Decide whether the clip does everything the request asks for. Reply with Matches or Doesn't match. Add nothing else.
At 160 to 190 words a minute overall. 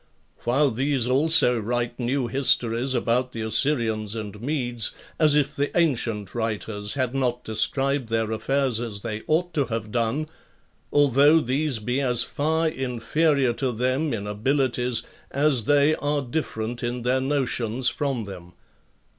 Doesn't match